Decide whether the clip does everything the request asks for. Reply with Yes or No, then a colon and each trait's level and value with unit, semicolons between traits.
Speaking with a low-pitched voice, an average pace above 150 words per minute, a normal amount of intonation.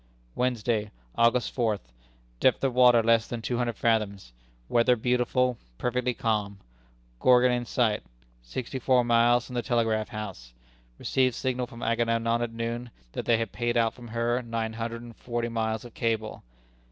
No: low, 115 Hz; average, 160 wpm; narrow, 1.5 semitones